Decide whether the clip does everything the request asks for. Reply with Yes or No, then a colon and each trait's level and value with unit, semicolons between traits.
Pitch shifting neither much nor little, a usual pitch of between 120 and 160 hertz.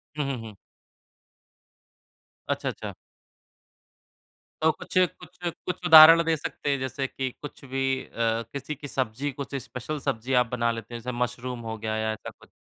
Yes: average, 3.7 semitones; low, 135 Hz